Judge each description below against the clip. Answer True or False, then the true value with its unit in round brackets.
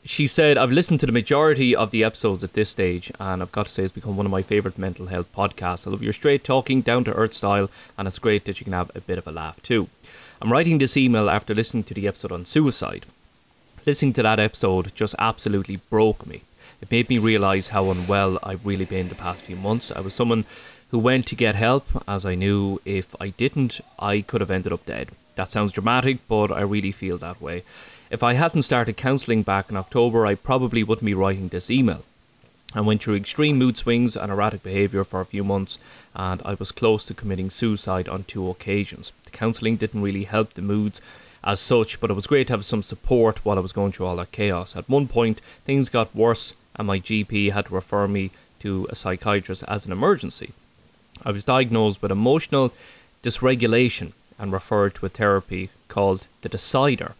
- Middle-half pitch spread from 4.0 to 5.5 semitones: False (3.4 semitones)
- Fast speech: True (215 wpm)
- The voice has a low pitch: True (105 Hz)